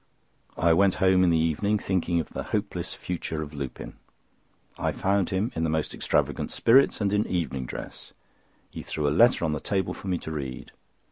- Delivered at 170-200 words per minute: Yes, average, 190 wpm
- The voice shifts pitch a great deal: No, average, 4.0 semitones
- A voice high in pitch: No, very low, 85 Hz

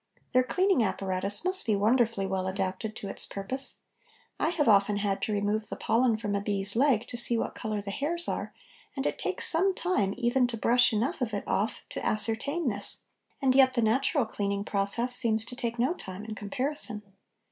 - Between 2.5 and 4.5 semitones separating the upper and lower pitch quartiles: Yes, average, 4.1 semitones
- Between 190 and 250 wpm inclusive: Yes, average, 200 wpm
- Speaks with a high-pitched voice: Yes, high, 225 Hz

